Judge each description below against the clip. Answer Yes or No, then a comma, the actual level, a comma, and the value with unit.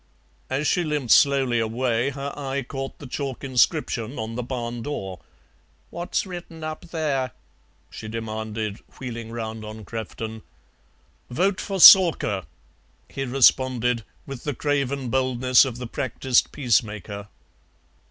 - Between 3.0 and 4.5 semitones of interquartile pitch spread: Yes, average, 3.6 semitones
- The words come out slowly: Yes, slow, 125 wpm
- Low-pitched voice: Yes, low, 125 Hz